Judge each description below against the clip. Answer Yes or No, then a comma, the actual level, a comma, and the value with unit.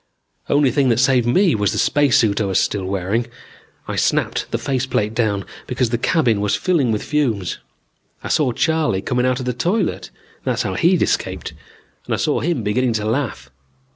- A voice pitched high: No, low, 120 Hz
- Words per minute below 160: No, average, 190 wpm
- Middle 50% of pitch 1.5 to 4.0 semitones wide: No, average, 5.3 semitones